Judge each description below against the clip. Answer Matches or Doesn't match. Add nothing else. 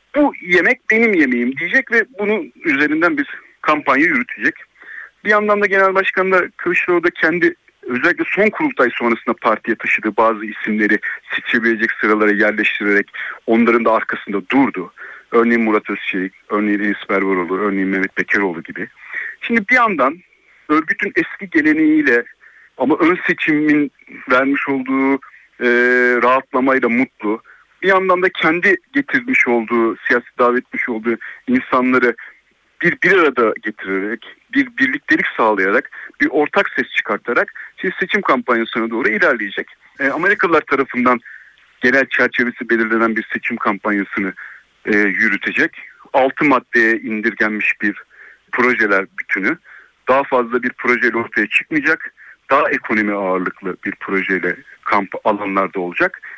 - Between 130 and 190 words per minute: Doesn't match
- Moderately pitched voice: Doesn't match